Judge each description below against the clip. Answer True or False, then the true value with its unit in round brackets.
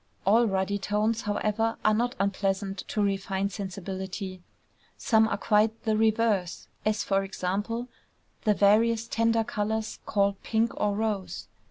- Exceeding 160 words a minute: False (135 wpm)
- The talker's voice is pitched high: True (210 Hz)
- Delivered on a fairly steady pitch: True (2.2 semitones)